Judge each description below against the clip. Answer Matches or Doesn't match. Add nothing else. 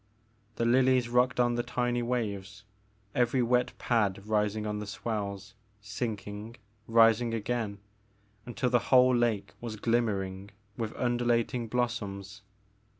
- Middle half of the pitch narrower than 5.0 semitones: Matches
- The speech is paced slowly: Matches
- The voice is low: Matches